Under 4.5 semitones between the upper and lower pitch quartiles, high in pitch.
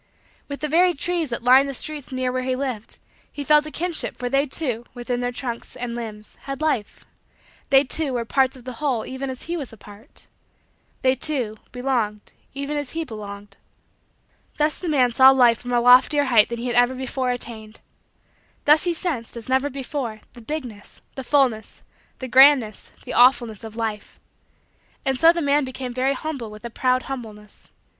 Yes: average, 3.2 semitones; very high, 255 Hz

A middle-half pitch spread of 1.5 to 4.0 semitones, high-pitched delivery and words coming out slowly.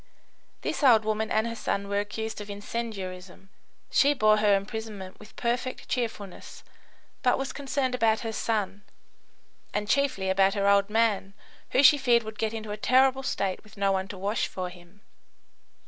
No: average, 2.9 semitones; high, 215 Hz; average, 170 wpm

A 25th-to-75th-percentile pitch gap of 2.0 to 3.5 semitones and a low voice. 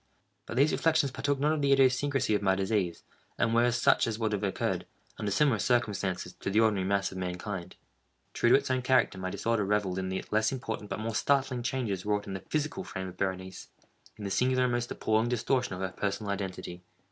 No: average, 4.8 semitones; low, 110 Hz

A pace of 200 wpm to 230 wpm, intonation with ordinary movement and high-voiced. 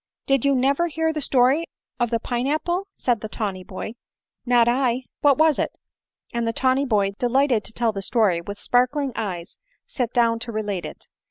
Yes: fast, 205 wpm; average, 4.0 semitones; high, 245 Hz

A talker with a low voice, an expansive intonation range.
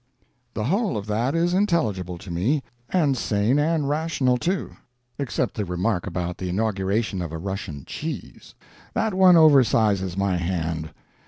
Yes: low, 110 Hz; wide, 8.7 semitones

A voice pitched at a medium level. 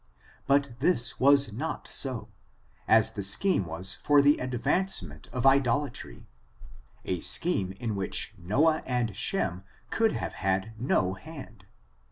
No: low, 120 Hz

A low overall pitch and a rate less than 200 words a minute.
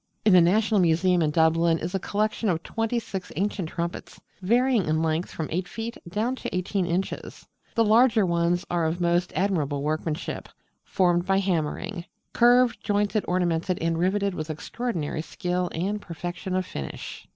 No: medium, 180 Hz; average, 160 wpm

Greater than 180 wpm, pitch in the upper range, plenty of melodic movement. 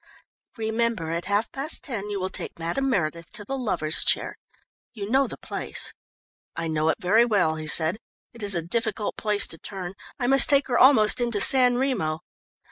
Yes: average, 190 wpm; high, 210 Hz; wide, 6.1 semitones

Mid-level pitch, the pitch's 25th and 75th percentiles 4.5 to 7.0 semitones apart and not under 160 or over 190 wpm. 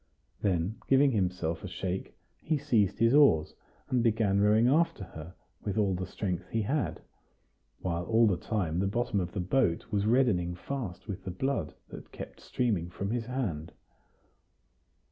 No: low, 100 Hz; average, 5.1 semitones; average, 165 wpm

